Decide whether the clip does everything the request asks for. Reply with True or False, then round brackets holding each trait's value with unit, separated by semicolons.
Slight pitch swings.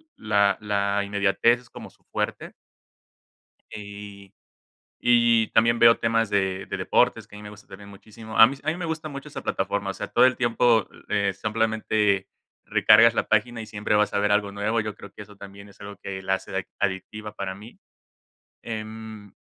True (2.0 semitones)